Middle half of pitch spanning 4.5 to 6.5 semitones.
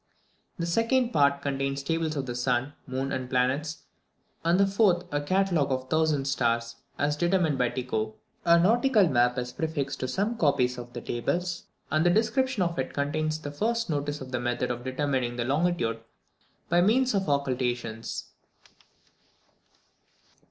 Yes: wide, 5.5 semitones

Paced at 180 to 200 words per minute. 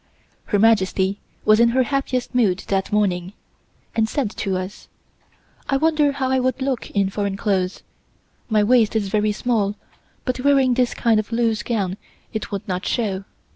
No: average, 170 wpm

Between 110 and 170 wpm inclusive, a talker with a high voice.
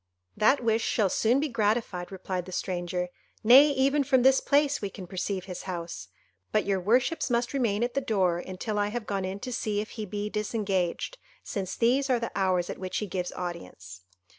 No: average, 200 wpm; high, 210 Hz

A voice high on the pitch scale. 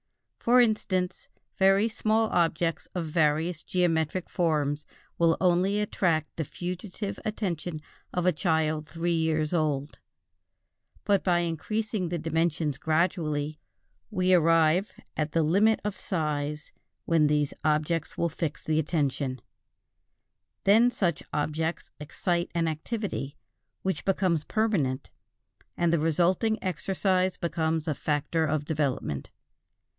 No: medium, 165 Hz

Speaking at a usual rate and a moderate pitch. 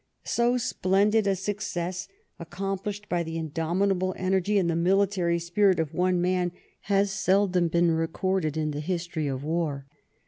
Yes: average, 150 wpm; medium, 180 Hz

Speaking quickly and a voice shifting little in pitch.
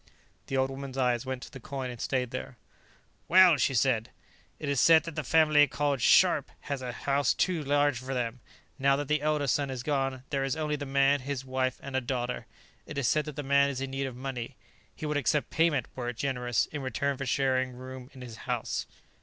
Yes: fast, 225 wpm; narrow, 2.0 semitones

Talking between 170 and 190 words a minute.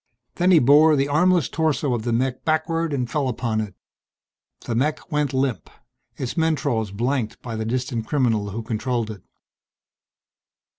No: average, 155 wpm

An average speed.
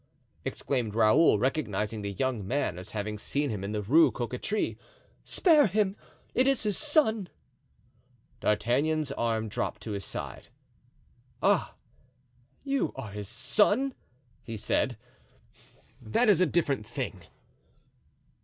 No: slow, 125 wpm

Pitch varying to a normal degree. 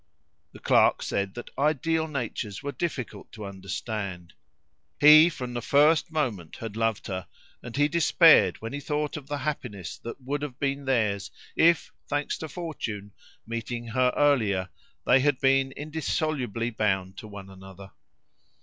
No: wide, 6.1 semitones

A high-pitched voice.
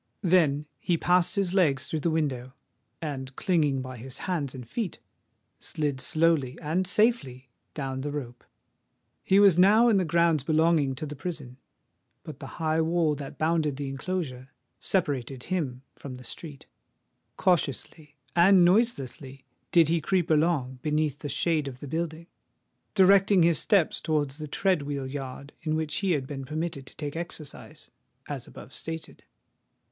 No: medium, 155 Hz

